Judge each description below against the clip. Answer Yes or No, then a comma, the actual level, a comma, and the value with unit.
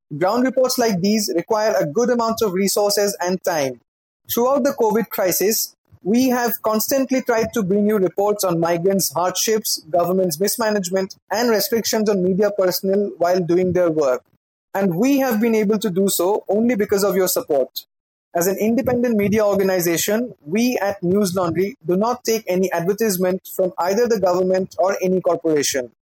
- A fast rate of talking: No, average, 165 wpm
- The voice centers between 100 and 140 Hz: No, high, 200 Hz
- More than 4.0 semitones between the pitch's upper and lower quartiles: No, average, 3.4 semitones